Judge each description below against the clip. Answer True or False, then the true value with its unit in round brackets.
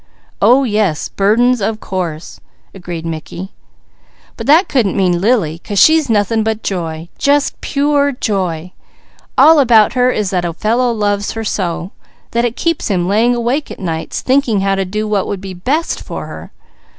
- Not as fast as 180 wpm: True (170 wpm)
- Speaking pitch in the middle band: False (210 Hz)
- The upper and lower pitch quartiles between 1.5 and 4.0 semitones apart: False (5.1 semitones)